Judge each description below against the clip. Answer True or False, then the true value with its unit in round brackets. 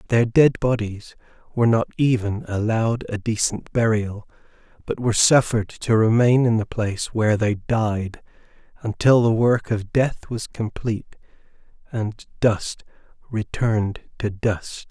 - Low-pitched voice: True (110 Hz)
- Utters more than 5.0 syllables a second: False (4.4 syllables/s)